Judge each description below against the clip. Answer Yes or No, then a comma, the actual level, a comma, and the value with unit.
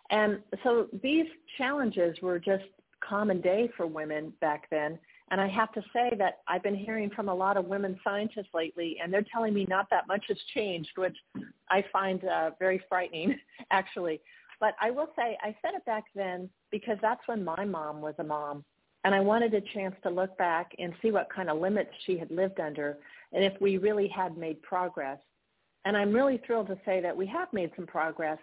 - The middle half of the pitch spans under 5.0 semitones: Yes, average, 3.7 semitones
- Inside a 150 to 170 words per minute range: No, fast, 205 wpm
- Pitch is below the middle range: No, high, 195 Hz